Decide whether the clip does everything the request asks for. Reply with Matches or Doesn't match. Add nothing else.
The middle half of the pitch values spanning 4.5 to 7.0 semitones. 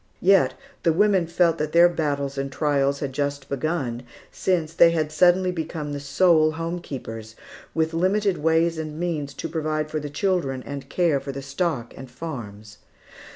Doesn't match